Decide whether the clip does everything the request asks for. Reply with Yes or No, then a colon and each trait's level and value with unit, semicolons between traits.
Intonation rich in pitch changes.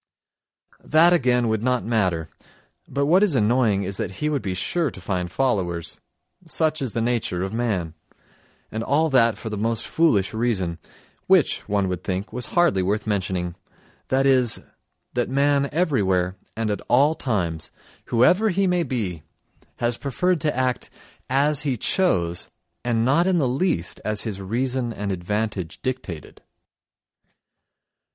Yes: wide, 6.4 semitones